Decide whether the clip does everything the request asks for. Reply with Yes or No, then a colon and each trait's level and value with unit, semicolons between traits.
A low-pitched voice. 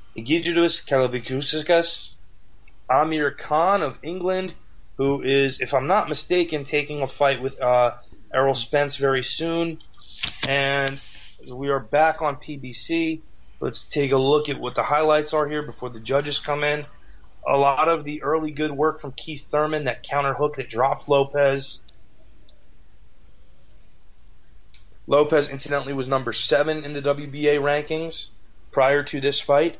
No: medium, 145 Hz